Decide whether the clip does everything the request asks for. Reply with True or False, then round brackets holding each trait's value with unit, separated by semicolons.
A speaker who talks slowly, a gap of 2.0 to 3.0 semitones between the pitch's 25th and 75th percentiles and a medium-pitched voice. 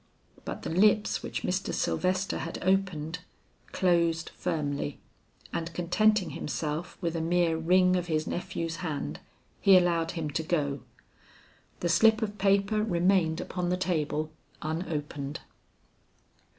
True (125 wpm; 2.6 semitones; 170 Hz)